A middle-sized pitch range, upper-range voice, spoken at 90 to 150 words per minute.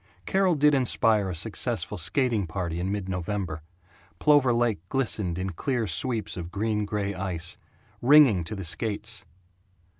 No: average, 4.7 semitones; low, 105 Hz; average, 145 wpm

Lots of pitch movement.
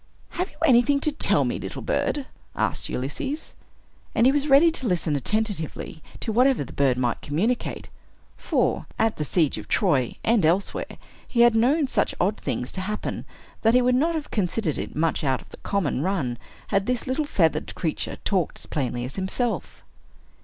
Yes: wide, 8.5 semitones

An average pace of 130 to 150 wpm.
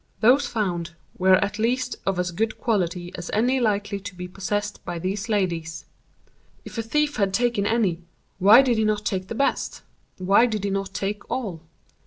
No: average, 180 wpm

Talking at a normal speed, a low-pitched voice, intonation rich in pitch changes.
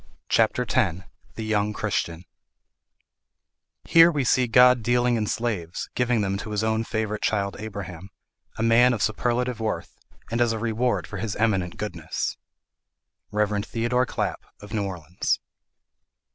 No: average, 145 wpm; low, 110 Hz; average, 3.0 semitones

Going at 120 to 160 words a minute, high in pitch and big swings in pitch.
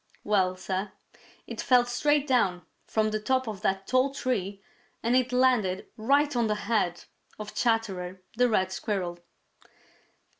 No: average, 145 wpm; high, 215 Hz; average, 4.7 semitones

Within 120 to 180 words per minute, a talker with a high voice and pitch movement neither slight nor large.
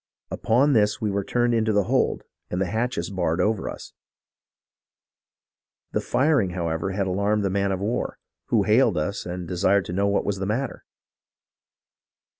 No: average, 165 wpm; low, 100 Hz; average, 3.0 semitones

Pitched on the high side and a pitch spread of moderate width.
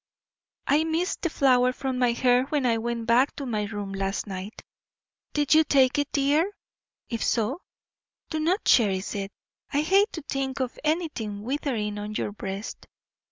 No: very high, 255 Hz; wide, 5.7 semitones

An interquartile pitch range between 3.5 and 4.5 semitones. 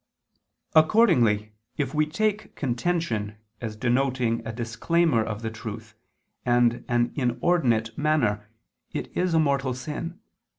No: wide, 5.4 semitones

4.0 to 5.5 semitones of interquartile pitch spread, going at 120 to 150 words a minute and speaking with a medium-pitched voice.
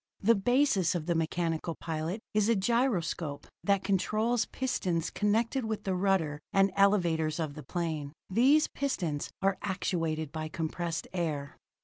Yes: average, 4.7 semitones; average, 140 wpm; medium, 180 Hz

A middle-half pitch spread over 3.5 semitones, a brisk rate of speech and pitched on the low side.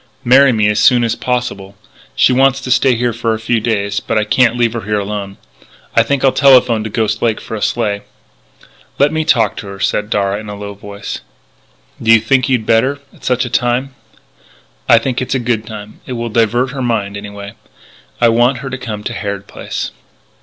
No: average, 3.2 semitones; fast, 210 wpm; low, 115 Hz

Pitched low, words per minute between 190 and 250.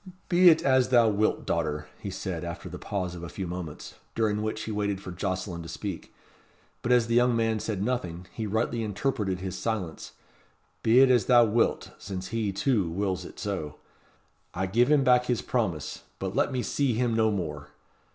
Yes: low, 105 Hz; average, 195 wpm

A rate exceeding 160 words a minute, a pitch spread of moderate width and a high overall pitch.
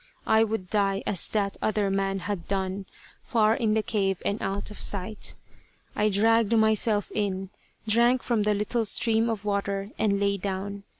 No: average, 170 wpm; narrow, 1.9 semitones; high, 205 Hz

